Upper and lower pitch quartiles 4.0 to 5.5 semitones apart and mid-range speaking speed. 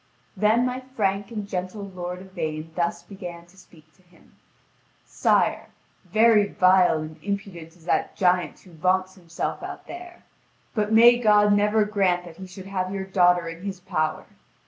No: average, 2.8 semitones; average, 165 wpm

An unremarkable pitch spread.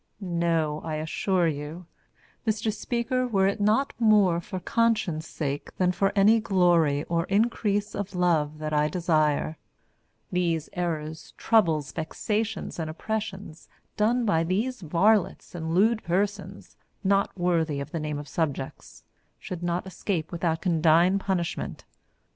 Yes: average, 4.2 semitones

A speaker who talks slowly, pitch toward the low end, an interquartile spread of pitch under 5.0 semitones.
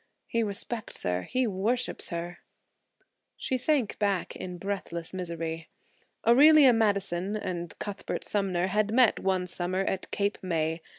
No: slow, 130 wpm; high, 195 Hz; average, 3.9 semitones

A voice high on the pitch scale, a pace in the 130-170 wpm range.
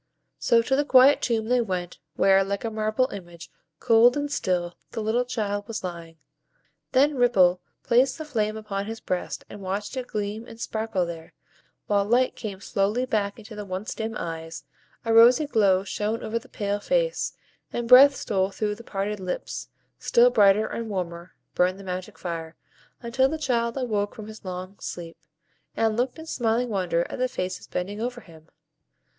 No: high, 215 Hz; average, 180 wpm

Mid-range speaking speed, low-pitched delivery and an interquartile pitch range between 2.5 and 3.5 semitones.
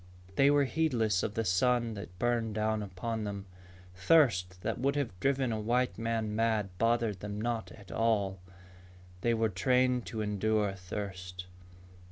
Yes: average, 155 wpm; low, 110 Hz; average, 3.0 semitones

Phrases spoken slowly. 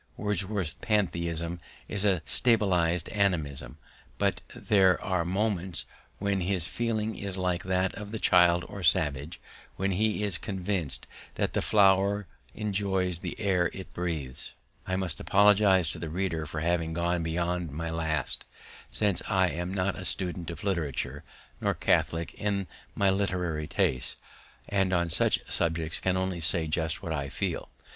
No: average, 150 wpm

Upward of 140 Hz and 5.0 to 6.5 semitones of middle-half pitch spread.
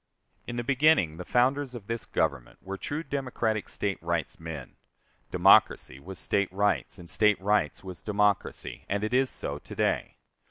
No: low, 105 Hz; wide, 5.4 semitones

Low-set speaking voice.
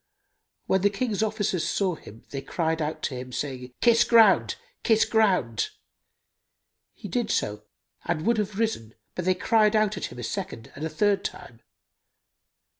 No: medium, 185 Hz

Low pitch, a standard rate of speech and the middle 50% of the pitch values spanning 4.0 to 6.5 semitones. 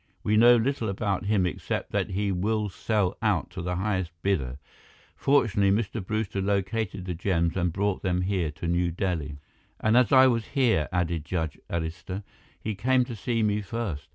No: low, 100 Hz; average, 180 wpm; average, 3.6 semitones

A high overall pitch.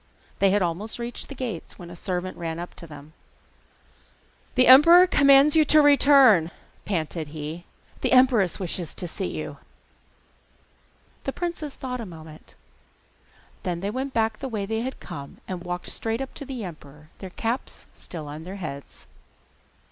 Yes: high, 195 Hz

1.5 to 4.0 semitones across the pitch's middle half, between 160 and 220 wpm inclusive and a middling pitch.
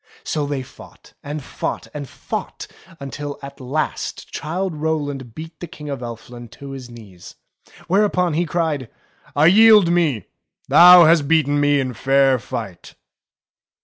No: average, 3.7 semitones; average, 145 wpm; medium, 145 Hz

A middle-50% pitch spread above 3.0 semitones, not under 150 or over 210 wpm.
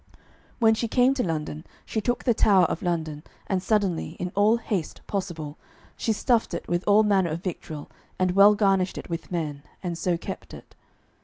Yes: average, 4.1 semitones; average, 185 wpm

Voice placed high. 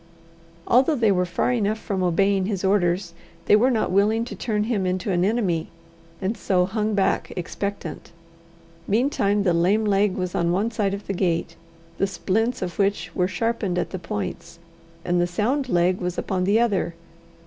Yes: high, 195 Hz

